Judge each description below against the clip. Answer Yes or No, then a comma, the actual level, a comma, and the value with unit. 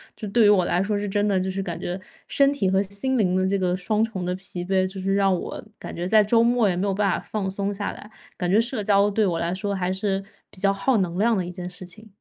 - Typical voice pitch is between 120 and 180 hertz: No, high, 195 Hz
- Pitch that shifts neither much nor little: No, narrow, 2.1 semitones